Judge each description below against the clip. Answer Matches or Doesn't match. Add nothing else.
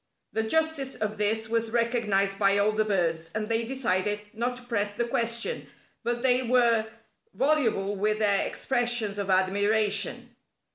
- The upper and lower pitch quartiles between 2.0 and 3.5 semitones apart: Matches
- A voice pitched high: Matches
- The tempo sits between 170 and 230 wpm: Doesn't match